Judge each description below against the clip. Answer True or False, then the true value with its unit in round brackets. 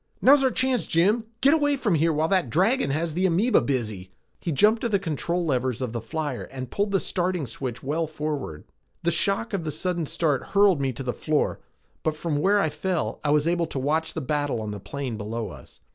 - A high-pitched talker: False (160 Hz)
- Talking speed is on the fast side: True (230 wpm)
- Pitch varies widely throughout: True (6.1 semitones)